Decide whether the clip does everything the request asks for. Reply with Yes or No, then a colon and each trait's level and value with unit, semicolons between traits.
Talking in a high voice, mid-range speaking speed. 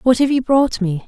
No: high, 240 Hz; fast, 280 wpm